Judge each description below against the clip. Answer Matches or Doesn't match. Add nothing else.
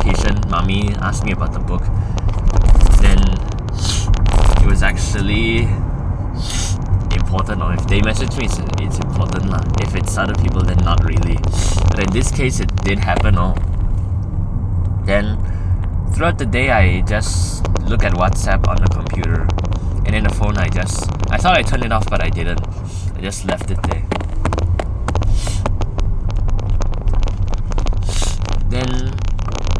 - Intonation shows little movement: Matches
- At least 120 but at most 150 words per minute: Matches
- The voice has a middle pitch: Doesn't match